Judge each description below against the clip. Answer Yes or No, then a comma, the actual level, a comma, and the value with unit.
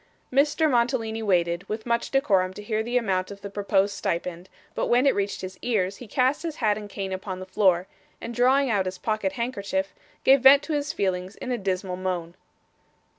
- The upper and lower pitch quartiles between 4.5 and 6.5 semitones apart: Yes, average, 4.8 semitones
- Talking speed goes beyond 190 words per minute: Yes, average, 200 wpm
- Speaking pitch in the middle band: No, high, 205 Hz